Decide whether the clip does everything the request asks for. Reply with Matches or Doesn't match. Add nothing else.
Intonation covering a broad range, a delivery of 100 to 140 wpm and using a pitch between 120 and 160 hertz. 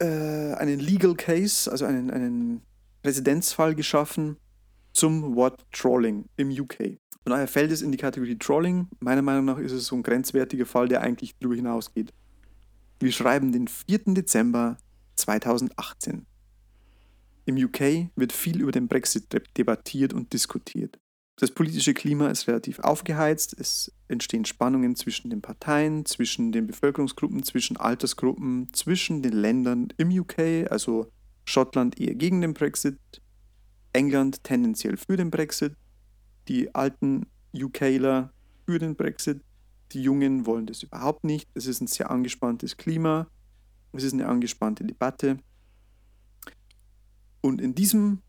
Matches